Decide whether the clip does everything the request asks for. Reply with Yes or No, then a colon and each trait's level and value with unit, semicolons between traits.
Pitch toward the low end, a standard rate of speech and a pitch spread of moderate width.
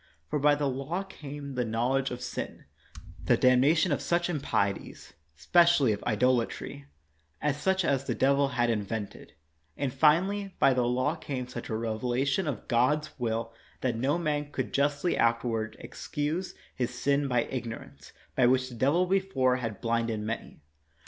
Yes: low, 130 Hz; average, 170 wpm; average, 4.0 semitones